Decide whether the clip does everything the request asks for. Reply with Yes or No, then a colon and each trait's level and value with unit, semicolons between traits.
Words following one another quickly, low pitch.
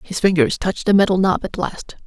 No: fast, 230 wpm; high, 190 Hz